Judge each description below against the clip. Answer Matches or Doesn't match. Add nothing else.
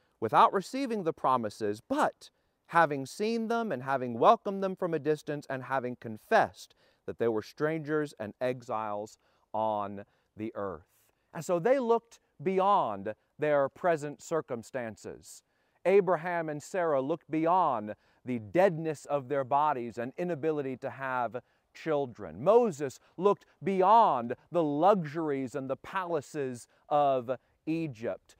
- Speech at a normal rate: Doesn't match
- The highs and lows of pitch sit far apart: Matches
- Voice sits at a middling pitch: Matches